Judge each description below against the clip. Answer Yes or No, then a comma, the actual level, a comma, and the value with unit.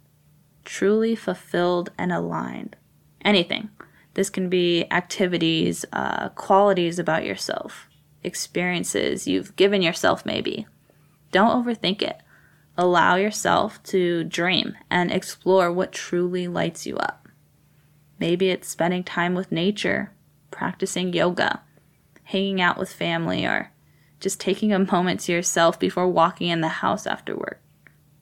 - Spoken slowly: Yes, slow, 125 wpm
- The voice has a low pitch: No, medium, 180 Hz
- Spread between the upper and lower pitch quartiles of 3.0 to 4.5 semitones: No, narrow, 2.6 semitones